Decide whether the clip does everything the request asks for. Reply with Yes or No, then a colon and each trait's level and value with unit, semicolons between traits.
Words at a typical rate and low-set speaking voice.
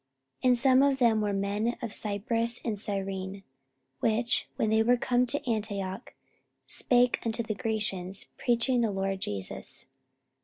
No: average, 150 wpm; high, 220 Hz